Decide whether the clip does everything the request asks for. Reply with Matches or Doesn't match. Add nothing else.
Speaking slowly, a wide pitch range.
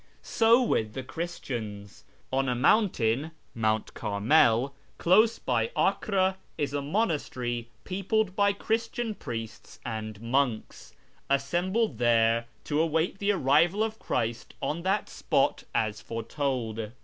Matches